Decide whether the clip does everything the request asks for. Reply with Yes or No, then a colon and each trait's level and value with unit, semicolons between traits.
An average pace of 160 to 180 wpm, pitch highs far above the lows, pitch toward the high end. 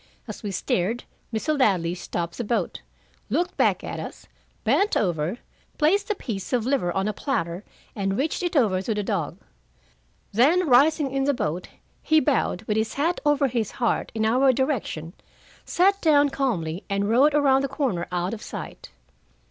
Yes: average, 175 wpm; wide, 6.9 semitones; high, 235 Hz